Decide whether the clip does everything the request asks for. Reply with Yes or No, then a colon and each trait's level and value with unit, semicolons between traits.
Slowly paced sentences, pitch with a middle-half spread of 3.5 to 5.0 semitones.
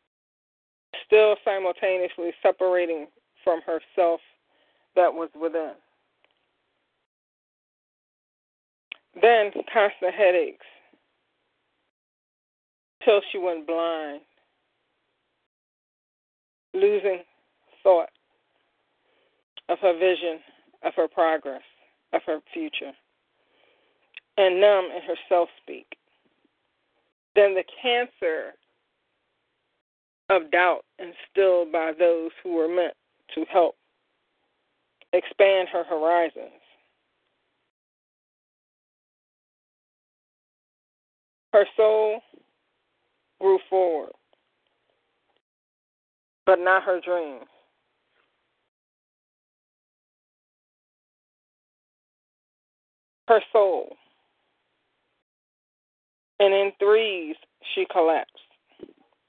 Yes: slow, 65 wpm; average, 4.0 semitones